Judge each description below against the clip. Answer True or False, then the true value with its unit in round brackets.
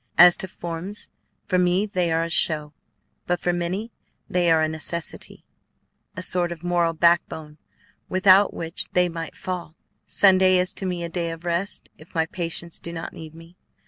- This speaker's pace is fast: False (175 wpm)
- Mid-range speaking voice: True (175 Hz)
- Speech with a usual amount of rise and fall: False (1.7 semitones)